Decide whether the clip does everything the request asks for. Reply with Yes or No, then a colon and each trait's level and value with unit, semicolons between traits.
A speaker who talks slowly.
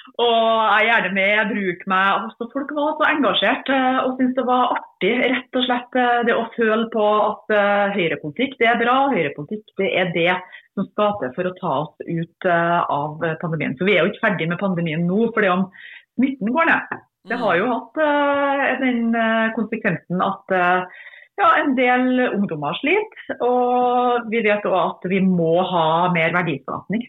No: average, 175 wpm